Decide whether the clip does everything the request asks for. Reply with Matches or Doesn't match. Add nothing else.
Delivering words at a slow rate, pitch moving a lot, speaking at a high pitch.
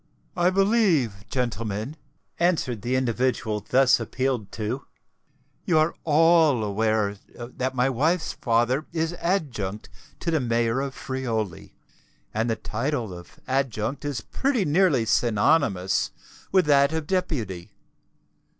Doesn't match